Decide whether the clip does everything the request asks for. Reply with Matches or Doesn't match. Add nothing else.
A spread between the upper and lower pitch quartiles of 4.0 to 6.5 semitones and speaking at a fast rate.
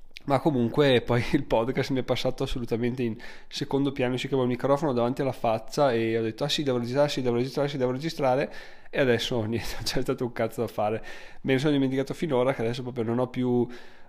Doesn't match